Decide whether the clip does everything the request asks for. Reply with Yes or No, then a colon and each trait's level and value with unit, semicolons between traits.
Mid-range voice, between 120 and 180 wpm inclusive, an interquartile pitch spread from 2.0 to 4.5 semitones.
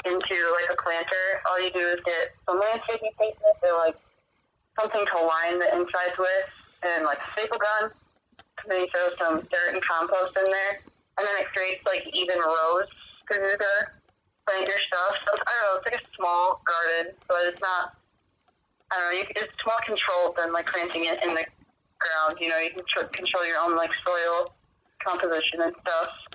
No: medium, 180 Hz; average, 200 wpm; average, 2.7 semitones